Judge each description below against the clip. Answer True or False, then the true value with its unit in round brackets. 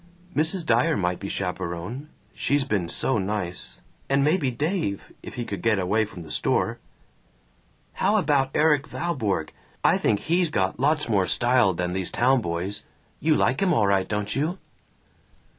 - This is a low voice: True (115 Hz)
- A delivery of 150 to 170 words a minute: True (160 wpm)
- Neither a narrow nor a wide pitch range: False (7.7 semitones)